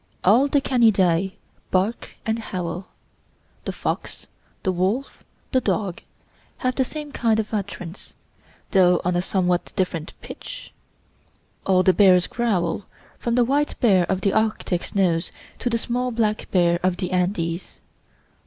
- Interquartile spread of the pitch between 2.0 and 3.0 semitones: No, average, 4.4 semitones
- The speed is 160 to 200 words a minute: No, average, 145 wpm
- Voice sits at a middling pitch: No, high, 195 Hz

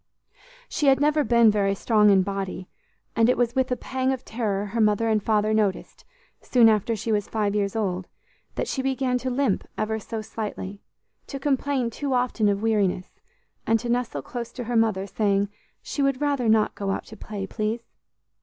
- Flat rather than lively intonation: No, average, 3.5 semitones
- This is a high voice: Yes, high, 220 Hz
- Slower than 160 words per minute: No, average, 190 wpm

